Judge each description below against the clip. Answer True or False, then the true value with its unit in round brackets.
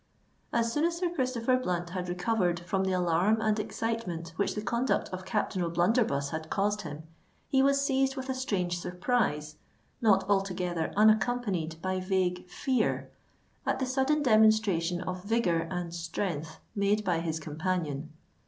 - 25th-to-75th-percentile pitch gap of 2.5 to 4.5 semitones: False (4.9 semitones)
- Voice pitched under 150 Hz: False (190 Hz)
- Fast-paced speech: False (155 wpm)